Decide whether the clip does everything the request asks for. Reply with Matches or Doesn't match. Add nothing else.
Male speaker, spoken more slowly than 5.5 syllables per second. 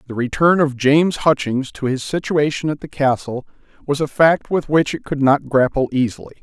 Matches